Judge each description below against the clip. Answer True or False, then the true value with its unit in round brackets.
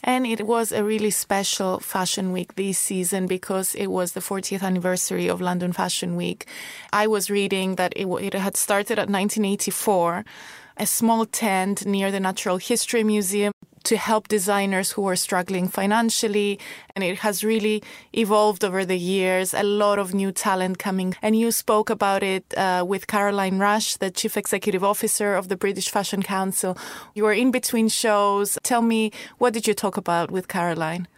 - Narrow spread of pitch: True (2.2 semitones)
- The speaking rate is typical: True (175 wpm)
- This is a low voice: False (200 Hz)